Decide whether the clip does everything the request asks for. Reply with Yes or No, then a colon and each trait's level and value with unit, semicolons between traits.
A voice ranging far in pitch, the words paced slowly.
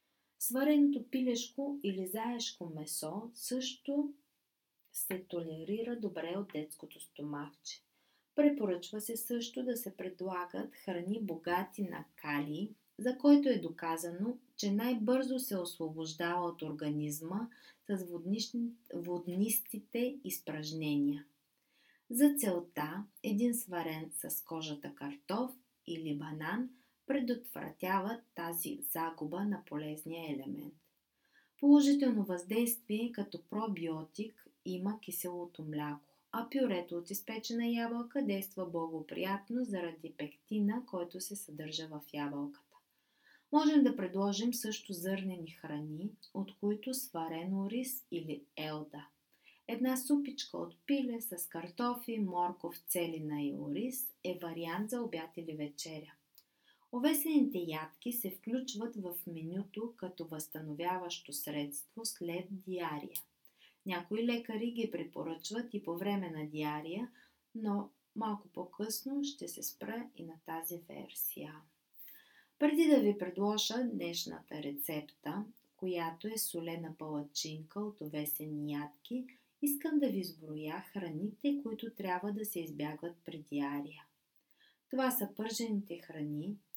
Yes: wide, 6.3 semitones; slow, 110 wpm